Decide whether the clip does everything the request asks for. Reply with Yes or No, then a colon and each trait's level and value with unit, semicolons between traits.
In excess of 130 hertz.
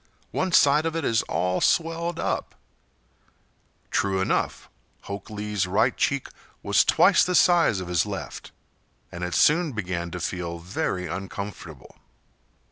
No: low, 100 Hz